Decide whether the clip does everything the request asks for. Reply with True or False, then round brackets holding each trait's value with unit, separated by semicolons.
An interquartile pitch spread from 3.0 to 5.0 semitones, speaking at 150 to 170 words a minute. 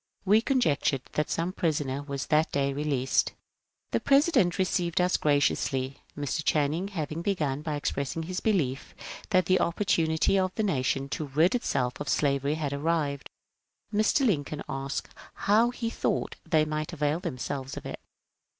True (4.6 semitones; 160 wpm)